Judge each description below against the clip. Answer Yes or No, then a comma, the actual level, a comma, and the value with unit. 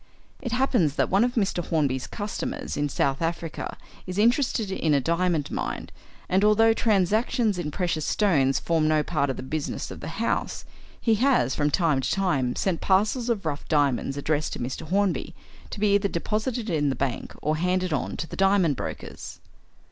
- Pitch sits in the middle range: Yes, medium, 175 Hz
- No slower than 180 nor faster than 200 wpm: Yes, average, 185 wpm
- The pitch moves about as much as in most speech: No, wide, 5.7 semitones